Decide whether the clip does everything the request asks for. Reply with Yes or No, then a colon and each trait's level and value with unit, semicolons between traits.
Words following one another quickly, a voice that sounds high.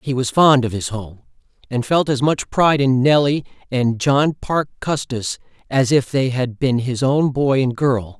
No: fast, 210 wpm; low, 130 Hz